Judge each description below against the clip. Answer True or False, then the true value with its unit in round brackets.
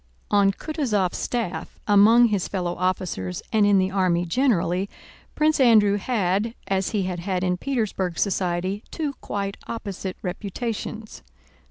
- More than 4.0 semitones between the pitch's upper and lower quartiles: False (3.4 semitones)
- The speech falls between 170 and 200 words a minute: False (135 wpm)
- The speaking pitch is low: False (200 Hz)